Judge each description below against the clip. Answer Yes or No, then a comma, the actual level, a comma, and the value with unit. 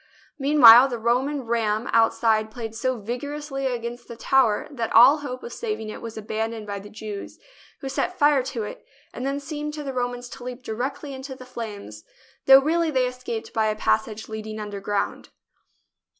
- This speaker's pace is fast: No, average, 180 wpm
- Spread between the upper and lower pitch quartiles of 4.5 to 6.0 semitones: No, average, 3.6 semitones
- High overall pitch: Yes, high, 245 Hz